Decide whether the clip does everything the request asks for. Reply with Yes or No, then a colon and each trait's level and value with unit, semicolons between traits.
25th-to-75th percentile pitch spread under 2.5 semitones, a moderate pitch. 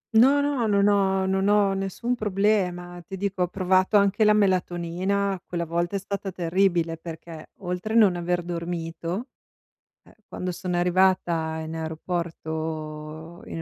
No: average, 2.8 semitones; medium, 180 Hz